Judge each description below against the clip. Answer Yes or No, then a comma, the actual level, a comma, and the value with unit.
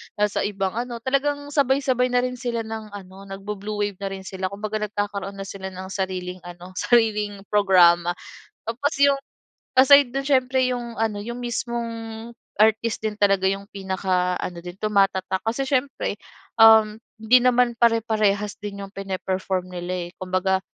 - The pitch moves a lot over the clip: No, average, 3.8 semitones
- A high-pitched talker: Yes, high, 205 Hz